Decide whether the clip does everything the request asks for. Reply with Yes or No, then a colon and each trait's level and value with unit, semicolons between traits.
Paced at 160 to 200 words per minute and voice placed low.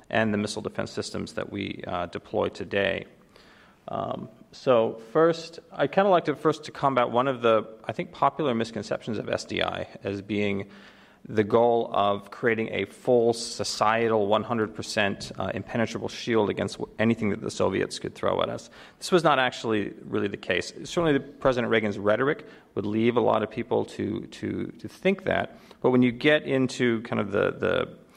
Yes: average, 180 wpm; low, 115 Hz